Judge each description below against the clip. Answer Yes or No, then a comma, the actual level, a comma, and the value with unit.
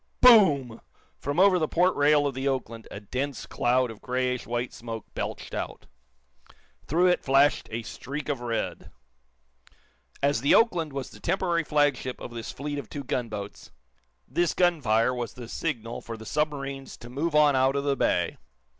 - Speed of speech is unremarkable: Yes, average, 170 wpm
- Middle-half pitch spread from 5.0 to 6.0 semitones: No, average, 3.8 semitones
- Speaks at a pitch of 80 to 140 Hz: Yes, low, 135 Hz